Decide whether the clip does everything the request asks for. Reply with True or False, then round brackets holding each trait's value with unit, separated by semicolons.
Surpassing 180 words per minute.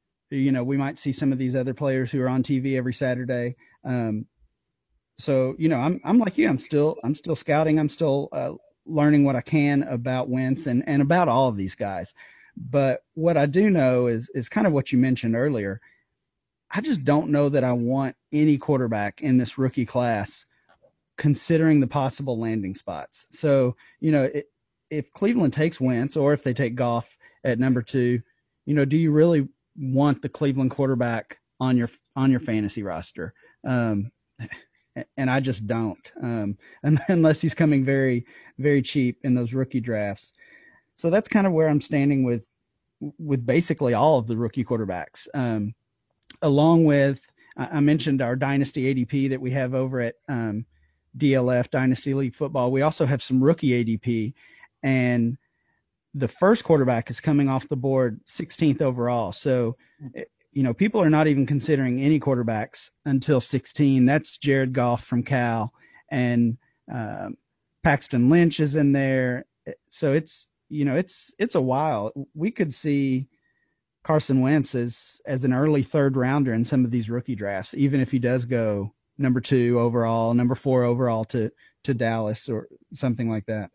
False (170 wpm)